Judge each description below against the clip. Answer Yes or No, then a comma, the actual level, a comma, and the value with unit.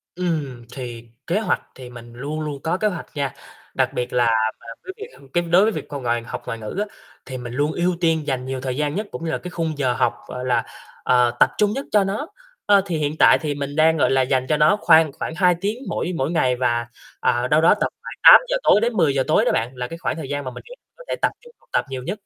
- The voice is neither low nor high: Yes, medium, 150 Hz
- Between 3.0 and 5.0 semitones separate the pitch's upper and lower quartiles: No, wide, 5.6 semitones